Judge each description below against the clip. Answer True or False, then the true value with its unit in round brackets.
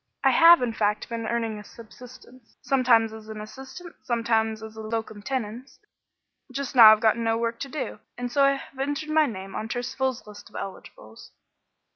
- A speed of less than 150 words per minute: False (180 wpm)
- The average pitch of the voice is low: False (230 Hz)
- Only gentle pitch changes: False (3.3 semitones)